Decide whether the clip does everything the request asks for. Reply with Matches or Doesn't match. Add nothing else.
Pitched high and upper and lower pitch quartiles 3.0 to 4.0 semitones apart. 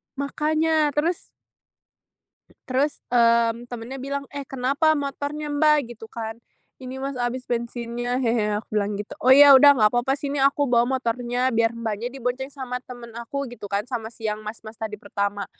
Matches